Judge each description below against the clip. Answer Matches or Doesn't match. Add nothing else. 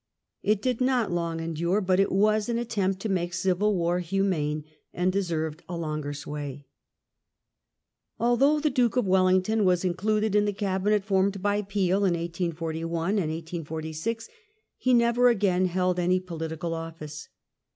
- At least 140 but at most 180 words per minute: Matches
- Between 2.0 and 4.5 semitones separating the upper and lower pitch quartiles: Matches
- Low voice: Doesn't match